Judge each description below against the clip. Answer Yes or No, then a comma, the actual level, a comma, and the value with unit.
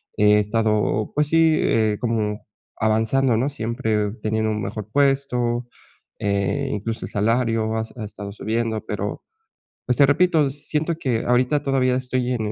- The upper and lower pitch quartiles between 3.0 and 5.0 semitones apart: Yes, average, 3.9 semitones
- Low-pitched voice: Yes, low, 115 Hz